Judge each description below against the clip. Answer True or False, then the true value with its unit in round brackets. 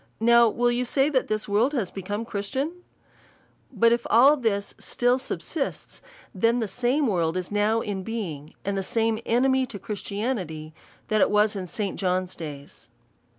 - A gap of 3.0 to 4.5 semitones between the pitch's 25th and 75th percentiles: True (3.9 semitones)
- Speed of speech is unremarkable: True (165 wpm)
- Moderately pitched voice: False (215 Hz)